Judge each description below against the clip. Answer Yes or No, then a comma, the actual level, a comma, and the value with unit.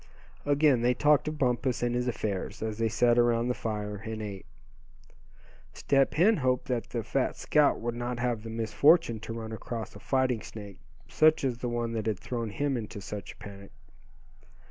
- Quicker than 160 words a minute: Yes, average, 190 wpm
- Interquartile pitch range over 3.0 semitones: No, narrow, 2.6 semitones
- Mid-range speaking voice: No, low, 120 Hz